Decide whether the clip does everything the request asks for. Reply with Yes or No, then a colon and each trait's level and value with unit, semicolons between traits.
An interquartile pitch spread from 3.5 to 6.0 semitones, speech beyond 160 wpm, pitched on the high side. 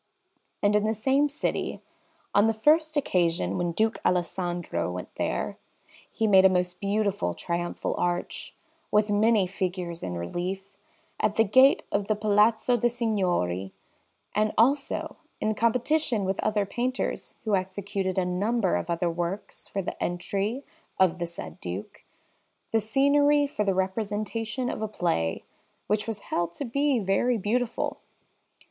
No: average, 4.0 semitones; average, 145 wpm; high, 205 Hz